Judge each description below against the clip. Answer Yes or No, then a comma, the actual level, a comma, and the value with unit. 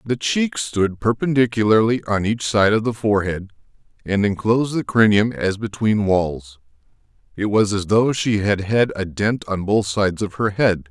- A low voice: Yes, low, 105 Hz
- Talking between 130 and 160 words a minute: No, average, 175 wpm